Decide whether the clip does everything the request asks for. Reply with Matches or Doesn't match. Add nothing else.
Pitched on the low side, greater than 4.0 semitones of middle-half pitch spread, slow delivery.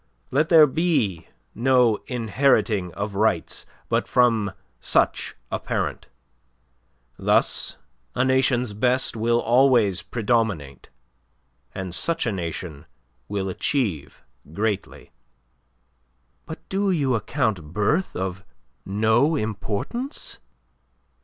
Matches